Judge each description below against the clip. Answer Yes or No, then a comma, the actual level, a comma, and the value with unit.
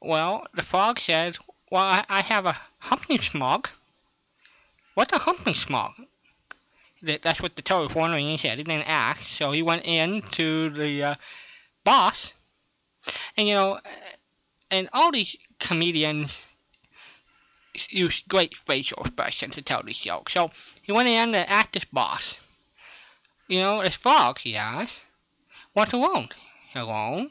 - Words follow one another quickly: No, average, 145 wpm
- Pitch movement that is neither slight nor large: Yes, average, 4.7 semitones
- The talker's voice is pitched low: No, medium, 180 Hz